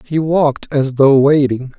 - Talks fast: No, average, 170 wpm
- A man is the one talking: Yes, male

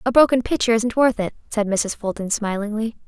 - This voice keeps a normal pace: Yes, average, 195 wpm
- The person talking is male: No, female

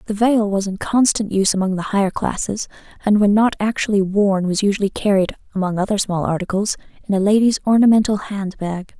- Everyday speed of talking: Yes, average, 185 wpm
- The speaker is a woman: Yes, female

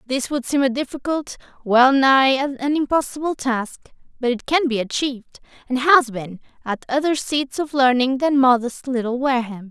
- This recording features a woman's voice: Yes, female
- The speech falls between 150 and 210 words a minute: Yes, average, 165 wpm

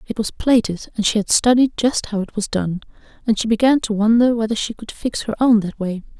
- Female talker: Yes, female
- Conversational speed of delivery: No, fast, 240 wpm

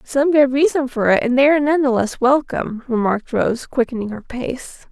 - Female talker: Yes, female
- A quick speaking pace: Yes, fast, 210 wpm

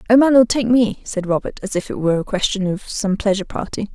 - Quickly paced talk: Yes, fast, 260 wpm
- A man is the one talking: No, female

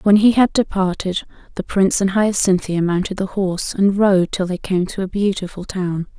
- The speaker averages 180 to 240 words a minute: Yes, average, 195 wpm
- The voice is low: No, high, 190 Hz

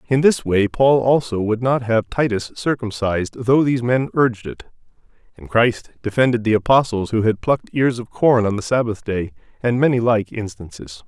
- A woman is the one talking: No, male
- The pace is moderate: Yes, average, 185 wpm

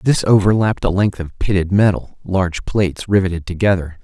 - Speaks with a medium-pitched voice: No, very low, 95 Hz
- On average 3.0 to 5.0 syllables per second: No, 5.6 syllables/s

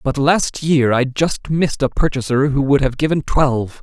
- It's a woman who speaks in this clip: No, male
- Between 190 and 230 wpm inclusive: Yes, fast, 205 wpm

